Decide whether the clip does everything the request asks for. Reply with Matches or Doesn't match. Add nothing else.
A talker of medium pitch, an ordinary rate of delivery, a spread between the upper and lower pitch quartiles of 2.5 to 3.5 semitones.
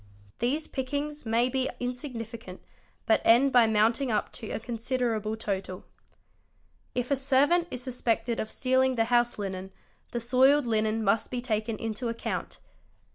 Doesn't match